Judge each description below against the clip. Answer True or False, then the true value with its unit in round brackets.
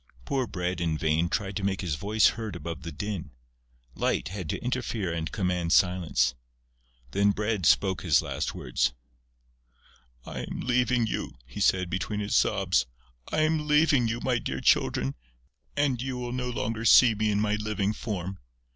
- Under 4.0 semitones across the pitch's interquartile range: False (5.2 semitones)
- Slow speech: False (170 wpm)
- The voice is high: False (100 Hz)